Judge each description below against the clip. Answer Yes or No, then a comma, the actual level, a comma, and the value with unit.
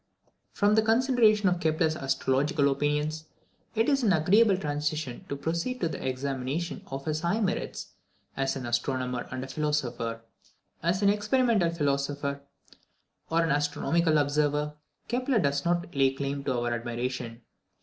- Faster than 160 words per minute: No, average, 150 wpm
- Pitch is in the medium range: Yes, medium, 150 Hz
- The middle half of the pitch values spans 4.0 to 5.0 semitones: Yes, average, 4.6 semitones